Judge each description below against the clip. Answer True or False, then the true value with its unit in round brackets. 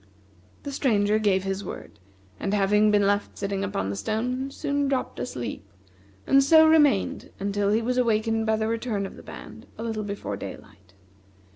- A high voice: True (215 Hz)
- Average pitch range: True (4.0 semitones)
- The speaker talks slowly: False (170 wpm)